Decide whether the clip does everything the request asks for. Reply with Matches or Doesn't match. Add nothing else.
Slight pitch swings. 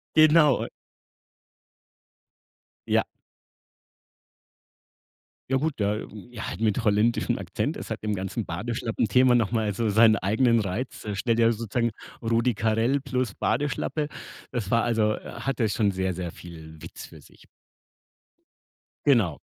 Doesn't match